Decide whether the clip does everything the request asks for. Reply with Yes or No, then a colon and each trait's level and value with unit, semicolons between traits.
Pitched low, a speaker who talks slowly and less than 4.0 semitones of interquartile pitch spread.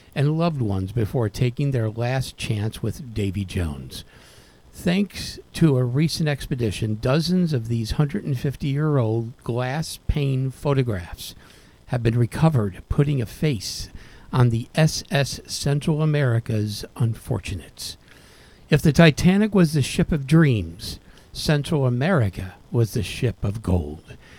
No: low, 125 Hz; slow, 130 wpm; wide, 5.6 semitones